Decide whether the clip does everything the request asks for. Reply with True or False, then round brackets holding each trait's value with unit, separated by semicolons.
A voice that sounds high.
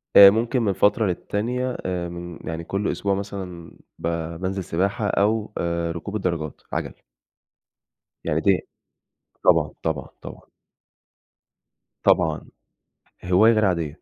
False (95 Hz)